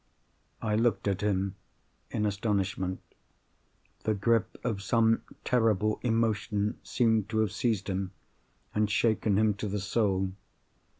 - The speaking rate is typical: No, slow, 125 wpm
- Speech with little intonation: Yes, narrow, 2.3 semitones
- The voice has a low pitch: Yes, low, 105 Hz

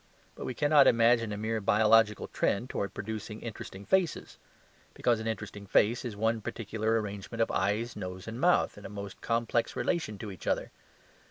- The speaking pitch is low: Yes, low, 110 Hz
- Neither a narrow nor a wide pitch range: No, narrow, 2.2 semitones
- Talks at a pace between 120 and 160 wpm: No, average, 175 wpm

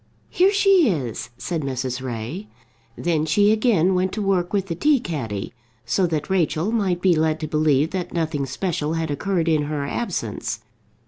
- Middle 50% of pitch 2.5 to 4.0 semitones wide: No, average, 4.6 semitones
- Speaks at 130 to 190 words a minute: Yes, average, 175 wpm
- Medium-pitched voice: Yes, medium, 165 Hz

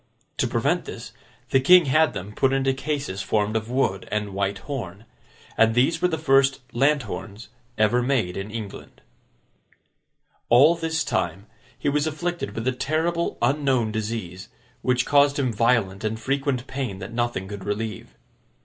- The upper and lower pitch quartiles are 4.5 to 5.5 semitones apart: Yes, average, 5.1 semitones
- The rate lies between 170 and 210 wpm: No, average, 155 wpm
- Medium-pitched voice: No, low, 120 Hz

